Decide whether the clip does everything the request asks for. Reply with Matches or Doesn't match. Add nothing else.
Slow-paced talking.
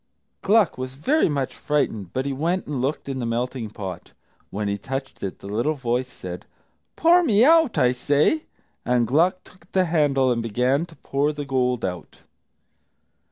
Doesn't match